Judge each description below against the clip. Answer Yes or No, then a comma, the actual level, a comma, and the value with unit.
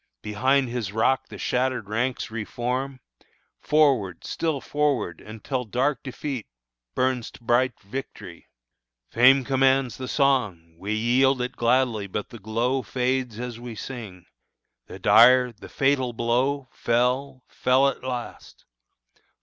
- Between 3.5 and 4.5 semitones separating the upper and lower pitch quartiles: No, narrow, 2.6 semitones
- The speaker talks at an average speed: No, slow, 130 wpm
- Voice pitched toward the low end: Yes, low, 125 Hz